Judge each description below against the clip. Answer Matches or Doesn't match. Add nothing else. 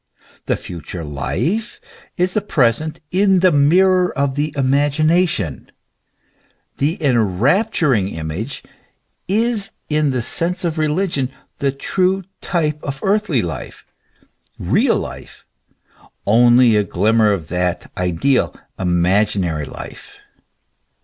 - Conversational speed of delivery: Doesn't match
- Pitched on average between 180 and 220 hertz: Doesn't match